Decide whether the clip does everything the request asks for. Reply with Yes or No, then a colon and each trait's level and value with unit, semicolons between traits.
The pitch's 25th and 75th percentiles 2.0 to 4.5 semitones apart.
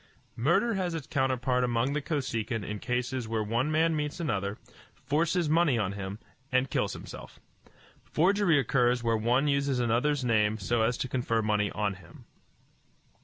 No: average, 4.9 semitones